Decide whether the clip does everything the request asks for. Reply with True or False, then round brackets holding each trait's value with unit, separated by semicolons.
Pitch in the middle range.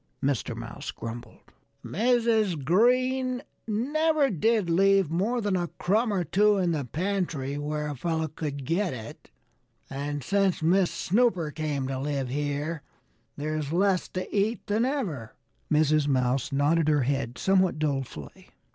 True (165 Hz)